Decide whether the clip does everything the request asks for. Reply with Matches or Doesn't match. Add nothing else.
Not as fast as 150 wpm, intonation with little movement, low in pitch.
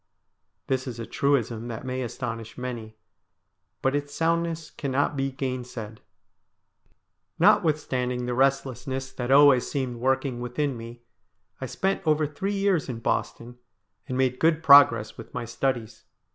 Doesn't match